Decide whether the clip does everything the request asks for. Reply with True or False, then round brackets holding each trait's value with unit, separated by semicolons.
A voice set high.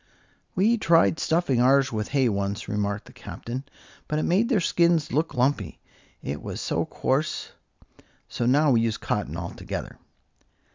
False (135 Hz)